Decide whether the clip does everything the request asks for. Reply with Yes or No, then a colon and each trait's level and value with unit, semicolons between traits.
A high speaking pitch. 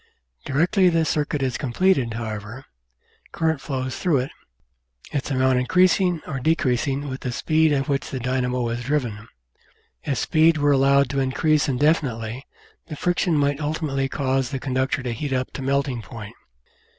No: low, 135 Hz